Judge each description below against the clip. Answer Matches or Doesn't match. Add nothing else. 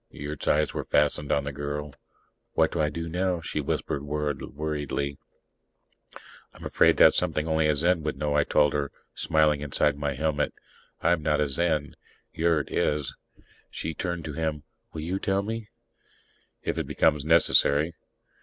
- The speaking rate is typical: Matches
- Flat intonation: Matches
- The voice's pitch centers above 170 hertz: Doesn't match